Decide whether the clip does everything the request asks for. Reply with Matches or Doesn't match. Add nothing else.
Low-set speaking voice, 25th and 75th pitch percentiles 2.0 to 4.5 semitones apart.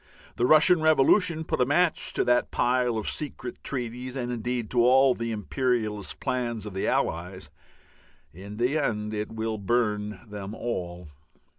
Matches